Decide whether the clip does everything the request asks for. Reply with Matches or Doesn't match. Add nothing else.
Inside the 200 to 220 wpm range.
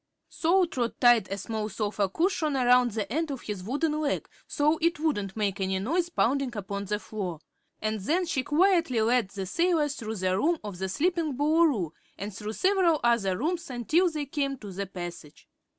Doesn't match